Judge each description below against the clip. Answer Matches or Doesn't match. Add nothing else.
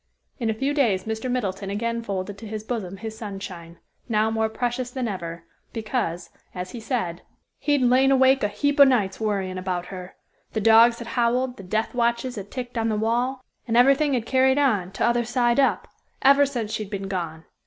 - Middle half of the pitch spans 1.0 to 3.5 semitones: Doesn't match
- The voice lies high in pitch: Matches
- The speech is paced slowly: Doesn't match